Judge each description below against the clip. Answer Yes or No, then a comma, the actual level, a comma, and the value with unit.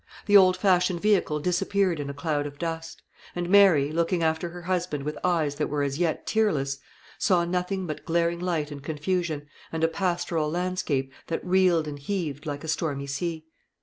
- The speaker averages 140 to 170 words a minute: No, average, 180 wpm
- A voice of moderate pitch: Yes, medium, 165 Hz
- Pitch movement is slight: No, average, 3.4 semitones